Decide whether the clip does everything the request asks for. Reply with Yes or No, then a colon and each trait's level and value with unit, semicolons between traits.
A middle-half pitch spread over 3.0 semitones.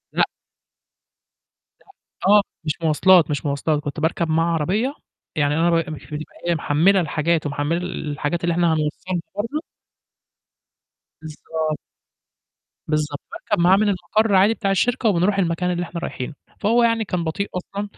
Yes: average, 4.1 semitones